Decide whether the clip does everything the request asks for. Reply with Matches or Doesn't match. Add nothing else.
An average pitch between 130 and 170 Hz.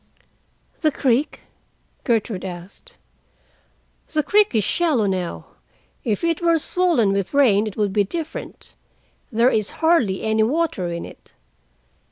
Doesn't match